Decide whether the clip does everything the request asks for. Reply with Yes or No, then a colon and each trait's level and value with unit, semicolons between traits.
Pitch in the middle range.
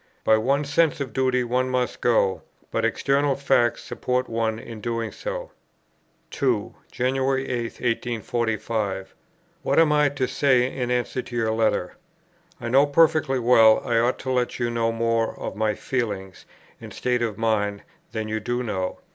No: low, 120 Hz